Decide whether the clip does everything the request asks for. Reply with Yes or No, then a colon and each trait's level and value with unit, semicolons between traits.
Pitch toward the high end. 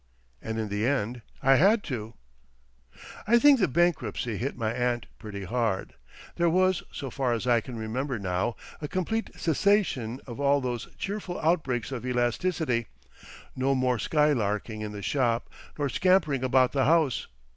No: low, 130 Hz